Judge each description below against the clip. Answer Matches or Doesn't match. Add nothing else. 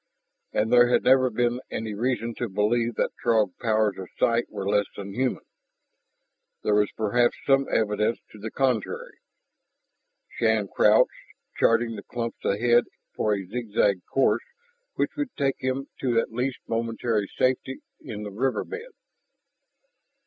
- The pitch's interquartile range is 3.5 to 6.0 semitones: Doesn't match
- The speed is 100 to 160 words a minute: Matches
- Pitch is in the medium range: Doesn't match